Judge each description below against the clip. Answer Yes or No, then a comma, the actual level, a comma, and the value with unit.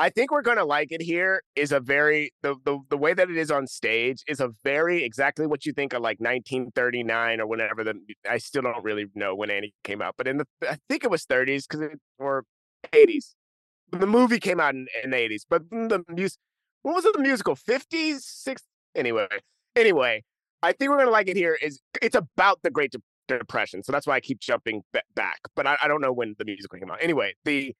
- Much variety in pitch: Yes, wide, 7.3 semitones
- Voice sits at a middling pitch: Yes, medium, 150 Hz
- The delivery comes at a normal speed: No, fast, 230 wpm